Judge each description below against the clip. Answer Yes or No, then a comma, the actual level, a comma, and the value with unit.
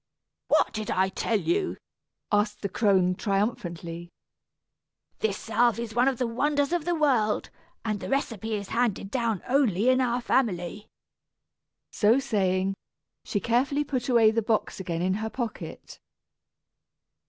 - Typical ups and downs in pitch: Yes, average, 4.2 semitones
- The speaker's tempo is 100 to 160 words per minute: Yes, average, 140 wpm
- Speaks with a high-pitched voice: Yes, high, 220 Hz